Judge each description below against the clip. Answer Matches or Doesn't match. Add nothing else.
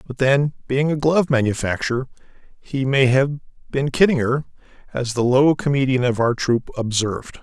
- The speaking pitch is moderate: Doesn't match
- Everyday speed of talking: Matches